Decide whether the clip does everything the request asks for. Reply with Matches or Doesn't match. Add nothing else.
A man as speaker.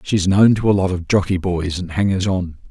Matches